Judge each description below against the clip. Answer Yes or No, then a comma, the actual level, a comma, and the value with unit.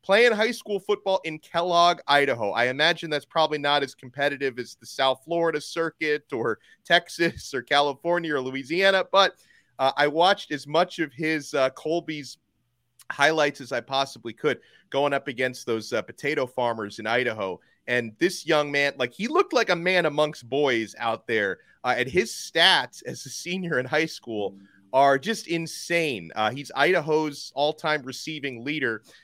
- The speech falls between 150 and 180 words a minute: Yes, average, 170 wpm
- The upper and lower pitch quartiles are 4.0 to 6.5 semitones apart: Yes, average, 4.5 semitones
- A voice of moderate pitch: Yes, medium, 150 Hz